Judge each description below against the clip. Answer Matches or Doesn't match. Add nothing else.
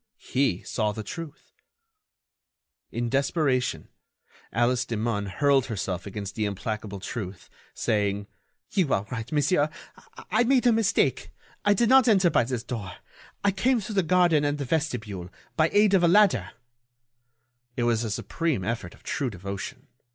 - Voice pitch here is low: Matches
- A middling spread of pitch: Doesn't match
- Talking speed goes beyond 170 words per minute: Doesn't match